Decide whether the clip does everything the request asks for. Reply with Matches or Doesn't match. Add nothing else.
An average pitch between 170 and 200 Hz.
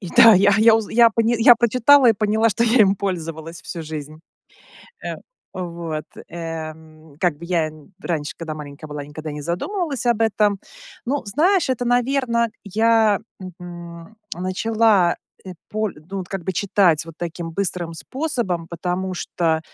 Matches